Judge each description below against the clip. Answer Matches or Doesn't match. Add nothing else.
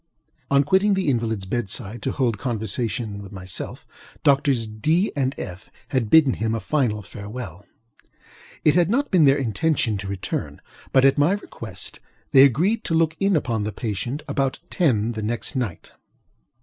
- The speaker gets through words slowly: Doesn't match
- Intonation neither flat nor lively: Doesn't match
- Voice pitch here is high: Doesn't match